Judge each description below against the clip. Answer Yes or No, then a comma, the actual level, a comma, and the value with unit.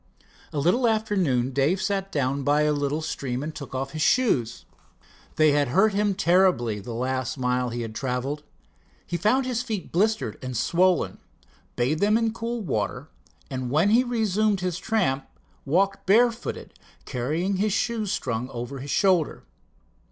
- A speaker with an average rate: Yes, average, 165 wpm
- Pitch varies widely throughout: Yes, wide, 7.8 semitones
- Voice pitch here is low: No, medium, 155 Hz